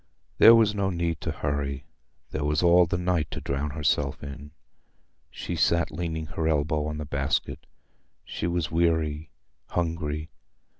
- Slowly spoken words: No, average, 145 wpm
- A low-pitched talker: Yes, very low, 80 Hz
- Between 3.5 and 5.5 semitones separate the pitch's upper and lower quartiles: No, average, 2.7 semitones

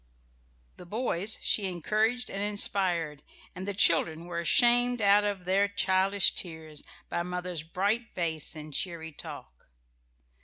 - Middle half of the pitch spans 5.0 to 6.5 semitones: No, average, 3.4 semitones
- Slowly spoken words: Yes, slow, 130 wpm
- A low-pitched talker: No, medium, 185 Hz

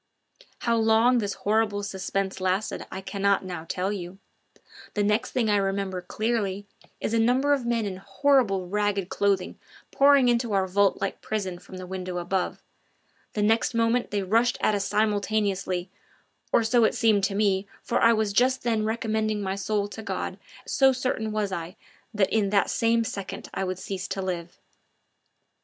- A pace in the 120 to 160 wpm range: No, average, 175 wpm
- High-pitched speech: Yes, high, 205 Hz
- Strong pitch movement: No, average, 2.7 semitones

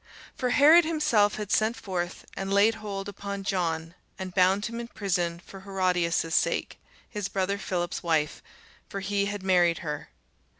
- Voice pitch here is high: Yes, high, 195 Hz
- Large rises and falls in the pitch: No, average, 2.8 semitones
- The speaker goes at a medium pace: Yes, average, 160 wpm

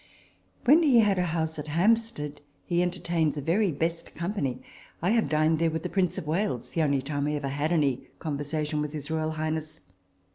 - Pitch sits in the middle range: Yes, medium, 160 Hz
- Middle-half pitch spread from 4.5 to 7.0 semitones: No, average, 3.0 semitones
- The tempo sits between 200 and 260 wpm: Yes, fast, 205 wpm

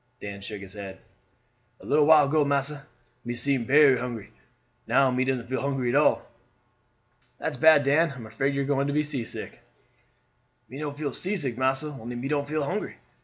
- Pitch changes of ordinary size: Yes, average, 3.2 semitones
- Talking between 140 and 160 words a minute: No, average, 190 wpm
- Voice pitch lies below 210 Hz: Yes, medium, 140 Hz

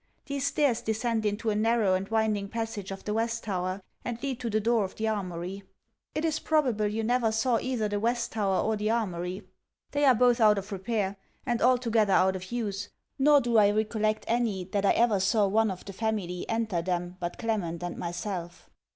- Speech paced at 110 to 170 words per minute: No, fast, 205 wpm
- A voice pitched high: Yes, high, 215 Hz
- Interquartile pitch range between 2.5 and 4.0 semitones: Yes, average, 3.1 semitones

